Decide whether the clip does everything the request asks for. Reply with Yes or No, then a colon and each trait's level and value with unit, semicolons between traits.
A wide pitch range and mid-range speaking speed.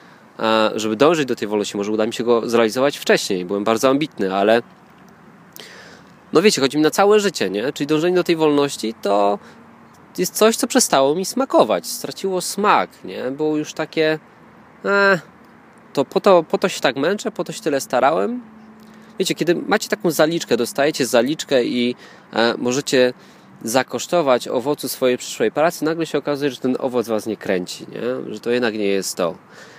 No: wide, 8.2 semitones; fast, 175 wpm